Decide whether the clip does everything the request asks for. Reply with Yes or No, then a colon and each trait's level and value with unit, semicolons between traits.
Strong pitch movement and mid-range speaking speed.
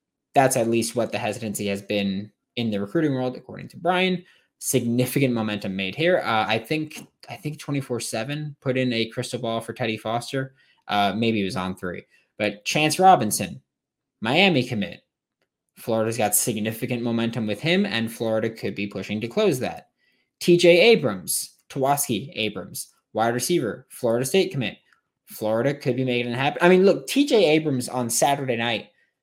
No: average, 4.7 semitones; average, 170 wpm